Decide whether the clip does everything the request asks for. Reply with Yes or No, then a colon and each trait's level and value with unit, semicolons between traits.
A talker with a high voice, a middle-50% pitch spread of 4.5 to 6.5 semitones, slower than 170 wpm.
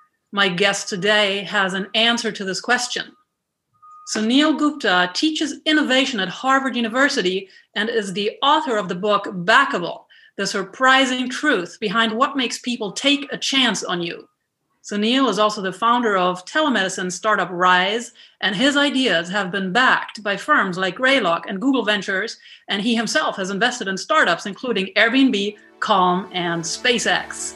Yes: high, 220 Hz; average, 5.2 semitones; average, 150 wpm